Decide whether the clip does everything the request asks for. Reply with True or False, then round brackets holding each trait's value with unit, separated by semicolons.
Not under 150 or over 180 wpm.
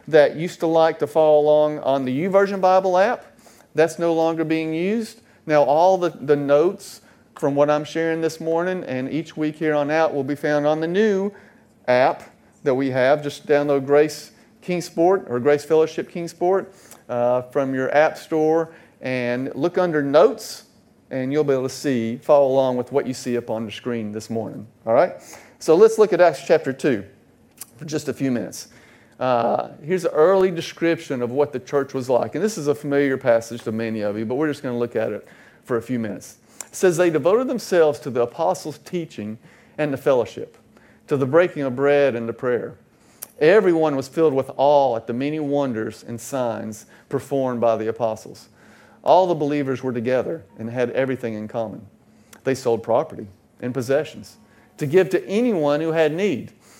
False (190 wpm)